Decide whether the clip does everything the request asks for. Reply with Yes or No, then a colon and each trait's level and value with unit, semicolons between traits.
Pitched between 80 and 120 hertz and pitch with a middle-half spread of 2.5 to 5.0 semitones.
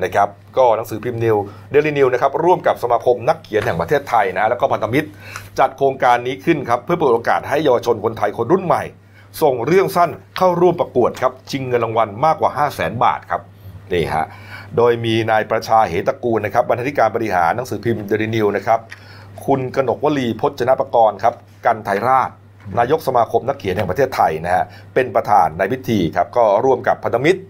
Yes: low, 115 Hz; average, 4.3 semitones